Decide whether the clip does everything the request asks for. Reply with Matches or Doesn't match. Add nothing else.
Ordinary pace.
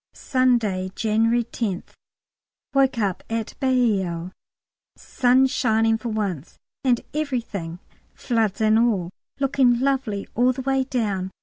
Doesn't match